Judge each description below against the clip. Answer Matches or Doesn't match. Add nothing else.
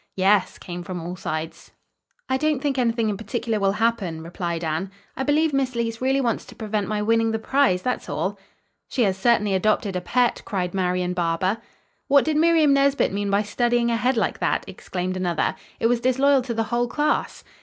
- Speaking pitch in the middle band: Doesn't match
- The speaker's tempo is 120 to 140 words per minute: Doesn't match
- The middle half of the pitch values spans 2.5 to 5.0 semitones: Doesn't match